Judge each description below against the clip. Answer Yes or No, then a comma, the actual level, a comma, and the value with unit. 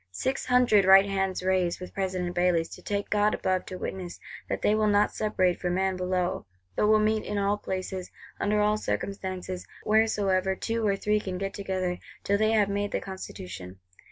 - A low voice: No, high, 195 Hz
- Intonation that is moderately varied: No, narrow, 2.3 semitones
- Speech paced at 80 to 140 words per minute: No, average, 185 wpm